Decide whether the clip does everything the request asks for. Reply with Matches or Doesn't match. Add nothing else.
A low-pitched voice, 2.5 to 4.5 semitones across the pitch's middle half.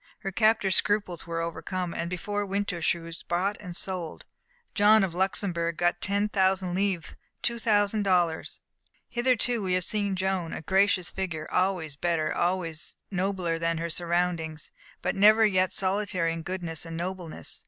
Doesn't match